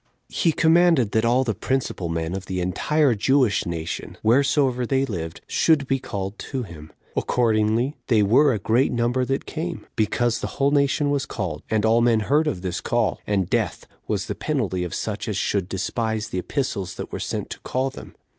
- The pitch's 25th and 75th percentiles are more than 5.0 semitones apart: Yes, wide, 5.5 semitones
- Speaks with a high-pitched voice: No, low, 115 Hz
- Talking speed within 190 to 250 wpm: Yes, average, 195 wpm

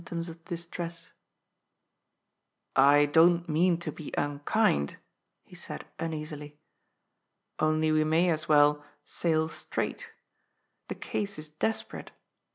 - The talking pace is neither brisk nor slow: No, slow, 125 wpm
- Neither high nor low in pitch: Yes, medium, 160 Hz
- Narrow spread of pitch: Yes, narrow, 2.3 semitones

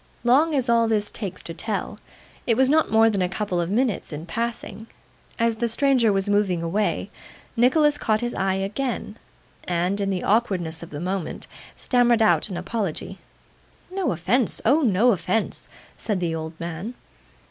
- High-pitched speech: Yes, high, 210 Hz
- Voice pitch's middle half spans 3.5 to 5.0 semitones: Yes, average, 4.6 semitones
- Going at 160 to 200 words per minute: Yes, average, 170 wpm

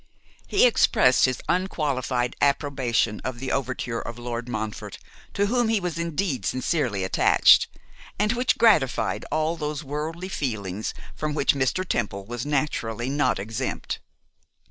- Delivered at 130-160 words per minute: Yes, slow, 135 wpm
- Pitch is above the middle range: No, low, 135 Hz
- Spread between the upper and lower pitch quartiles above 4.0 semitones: Yes, average, 5.3 semitones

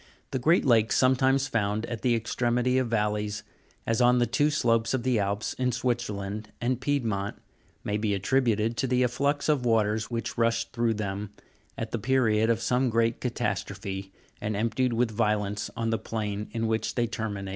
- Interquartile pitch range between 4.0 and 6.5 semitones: No, average, 2.9 semitones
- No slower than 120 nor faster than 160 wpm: No, average, 180 wpm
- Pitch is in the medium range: No, low, 115 Hz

